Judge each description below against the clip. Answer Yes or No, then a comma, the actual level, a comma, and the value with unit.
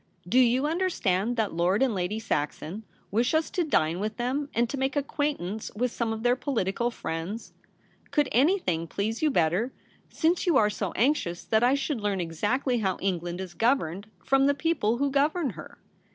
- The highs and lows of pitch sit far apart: Yes, wide, 6.5 semitones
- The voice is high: Yes, high, 230 Hz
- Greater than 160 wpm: Yes, average, 190 wpm